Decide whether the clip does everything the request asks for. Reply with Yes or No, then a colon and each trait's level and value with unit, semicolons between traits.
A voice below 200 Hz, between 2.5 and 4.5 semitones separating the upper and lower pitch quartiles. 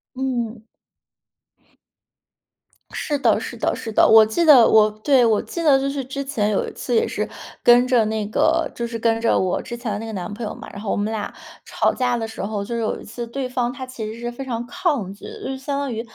No: high, 235 Hz; average, 3.4 semitones